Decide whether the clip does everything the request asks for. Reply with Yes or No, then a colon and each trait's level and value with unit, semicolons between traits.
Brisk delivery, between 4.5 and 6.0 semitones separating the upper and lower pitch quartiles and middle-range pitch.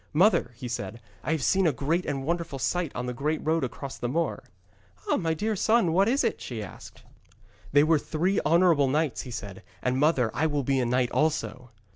Yes: fast, 210 wpm; average, 4.9 semitones; medium, 150 Hz